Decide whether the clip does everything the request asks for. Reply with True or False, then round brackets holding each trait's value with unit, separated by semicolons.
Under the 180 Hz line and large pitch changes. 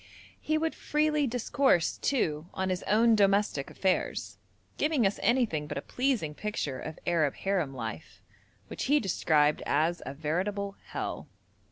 False (195 Hz; 7.8 semitones)